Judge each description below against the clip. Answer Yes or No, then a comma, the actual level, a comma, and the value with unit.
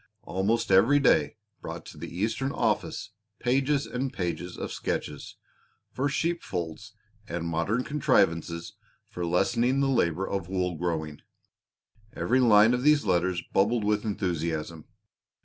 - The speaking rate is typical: No, slow, 130 wpm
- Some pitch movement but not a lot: No, wide, 6.3 semitones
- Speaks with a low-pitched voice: Yes, low, 100 Hz